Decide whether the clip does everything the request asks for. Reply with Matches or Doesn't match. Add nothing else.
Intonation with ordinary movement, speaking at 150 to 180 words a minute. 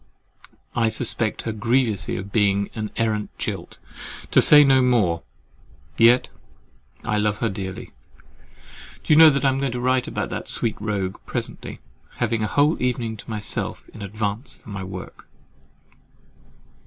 Doesn't match